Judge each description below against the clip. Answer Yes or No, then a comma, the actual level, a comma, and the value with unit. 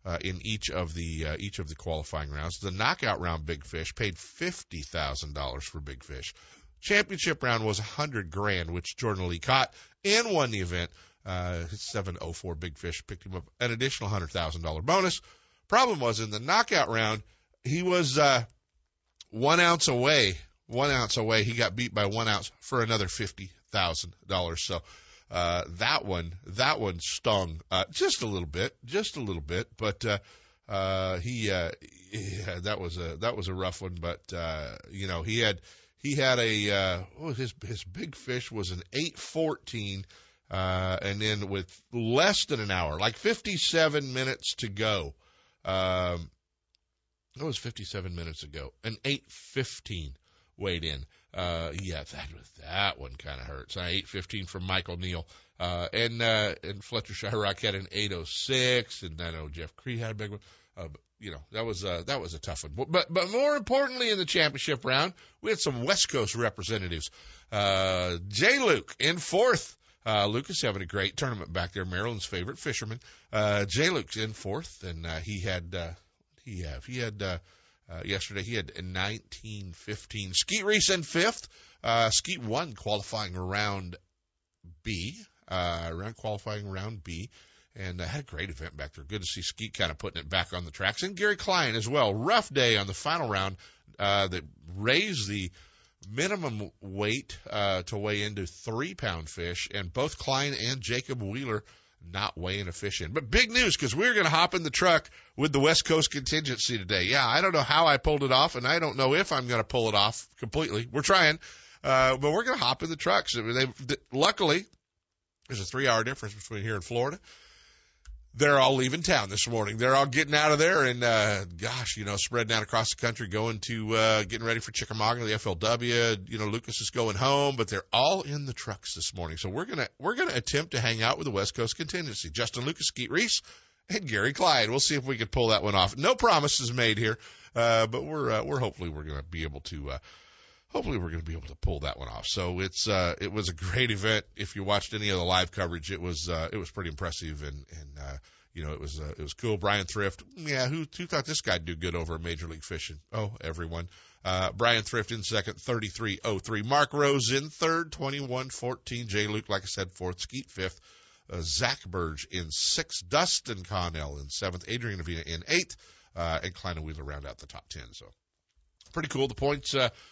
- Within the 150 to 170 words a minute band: No, fast, 205 wpm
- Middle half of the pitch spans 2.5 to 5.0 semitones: No, wide, 5.5 semitones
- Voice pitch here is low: Yes, low, 100 Hz